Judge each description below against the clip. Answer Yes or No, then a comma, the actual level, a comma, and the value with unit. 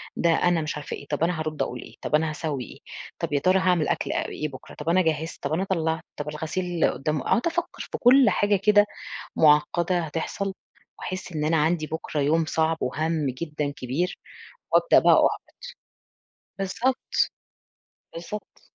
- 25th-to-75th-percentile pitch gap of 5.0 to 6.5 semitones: No, average, 3.3 semitones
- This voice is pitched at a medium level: Yes, medium, 160 Hz